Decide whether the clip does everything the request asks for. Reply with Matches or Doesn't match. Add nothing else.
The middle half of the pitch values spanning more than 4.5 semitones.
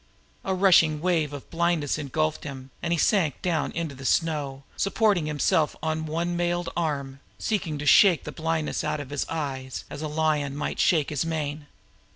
Doesn't match